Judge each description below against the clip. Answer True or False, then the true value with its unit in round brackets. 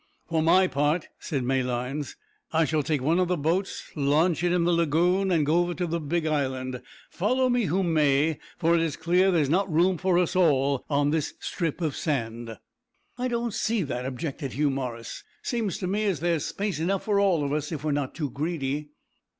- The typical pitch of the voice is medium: True (160 Hz)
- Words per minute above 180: True (205 wpm)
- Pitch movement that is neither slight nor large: True (4.1 semitones)